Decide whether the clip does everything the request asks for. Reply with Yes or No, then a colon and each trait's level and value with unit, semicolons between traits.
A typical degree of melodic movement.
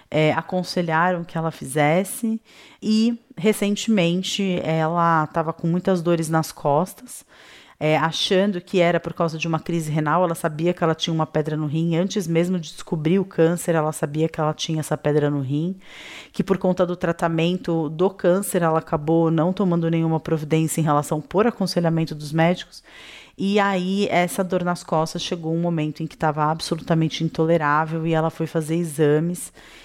No: narrow, 2.3 semitones